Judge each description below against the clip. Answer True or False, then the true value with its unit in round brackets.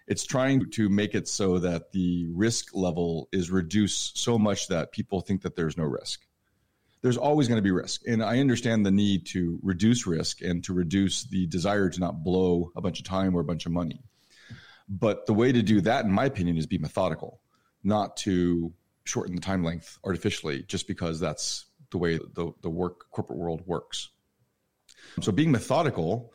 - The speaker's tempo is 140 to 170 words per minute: False (195 wpm)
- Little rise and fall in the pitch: False (3.6 semitones)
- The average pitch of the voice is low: True (95 Hz)